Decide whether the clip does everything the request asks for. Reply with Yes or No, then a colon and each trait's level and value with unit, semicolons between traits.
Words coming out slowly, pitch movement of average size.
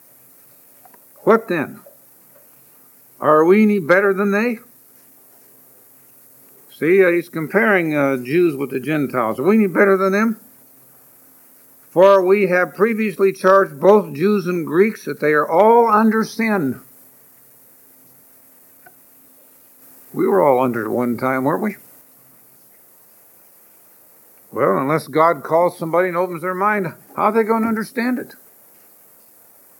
Yes: slow, 125 wpm; average, 5.0 semitones